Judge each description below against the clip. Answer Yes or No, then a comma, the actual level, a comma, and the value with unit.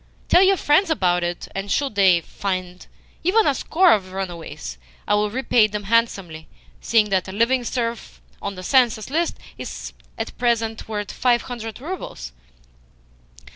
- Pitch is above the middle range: Yes, high, 220 Hz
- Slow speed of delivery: No, average, 160 wpm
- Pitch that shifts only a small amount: No, average, 5.2 semitones